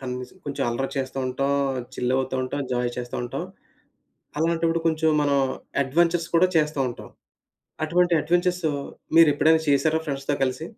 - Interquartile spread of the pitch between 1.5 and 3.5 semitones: No, average, 3.9 semitones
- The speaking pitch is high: No, medium, 145 Hz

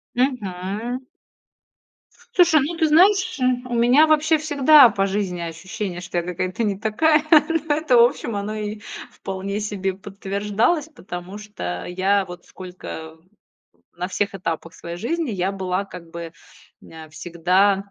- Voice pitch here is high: Yes, high, 200 Hz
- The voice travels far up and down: Yes, wide, 6.2 semitones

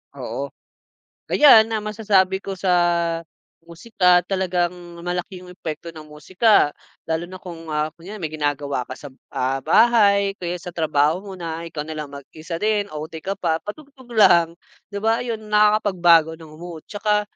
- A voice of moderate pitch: Yes, medium, 180 Hz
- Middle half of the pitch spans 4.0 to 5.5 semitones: Yes, average, 4.3 semitones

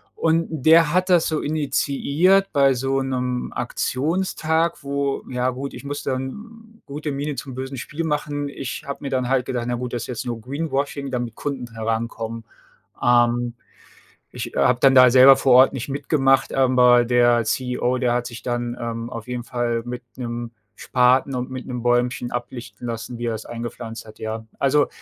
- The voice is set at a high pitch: No, low, 130 Hz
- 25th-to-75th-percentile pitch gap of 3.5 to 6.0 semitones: No, average, 2.7 semitones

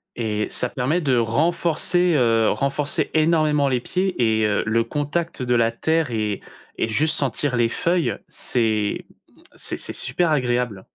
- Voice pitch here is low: Yes, low, 125 Hz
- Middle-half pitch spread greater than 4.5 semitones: Yes, wide, 5.4 semitones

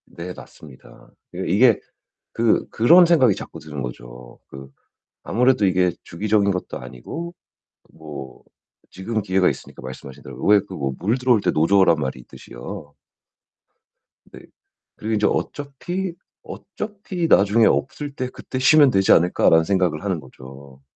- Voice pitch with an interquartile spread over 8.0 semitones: Yes, wide, 8.8 semitones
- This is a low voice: Yes, very low, 95 Hz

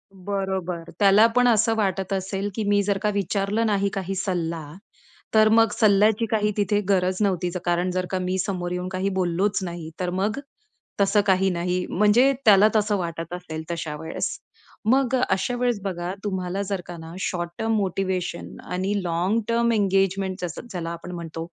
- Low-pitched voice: No, high, 190 Hz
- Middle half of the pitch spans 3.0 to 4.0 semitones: No, narrow, 2.6 semitones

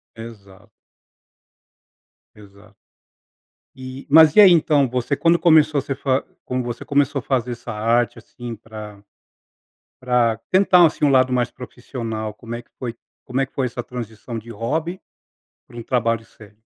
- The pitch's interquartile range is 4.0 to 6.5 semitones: No, average, 3.3 semitones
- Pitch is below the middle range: Yes, low, 125 Hz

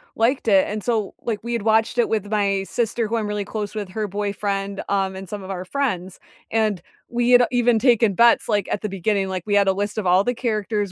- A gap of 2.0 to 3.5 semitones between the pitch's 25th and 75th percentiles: Yes, narrow, 2.6 semitones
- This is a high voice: Yes, high, 210 Hz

